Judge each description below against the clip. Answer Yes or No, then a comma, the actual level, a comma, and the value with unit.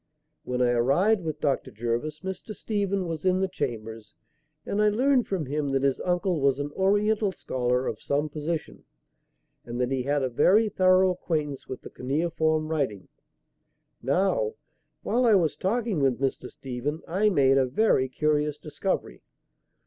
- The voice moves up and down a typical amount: No, wide, 6.1 semitones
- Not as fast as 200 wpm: Yes, average, 160 wpm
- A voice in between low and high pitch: Yes, medium, 155 Hz